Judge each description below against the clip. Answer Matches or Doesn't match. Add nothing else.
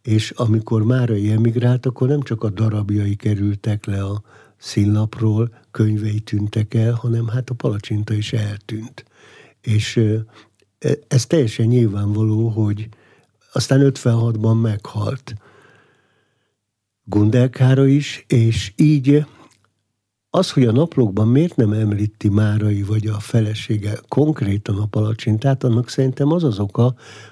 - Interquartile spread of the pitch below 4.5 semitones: Matches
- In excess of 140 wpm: Doesn't match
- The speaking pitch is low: Matches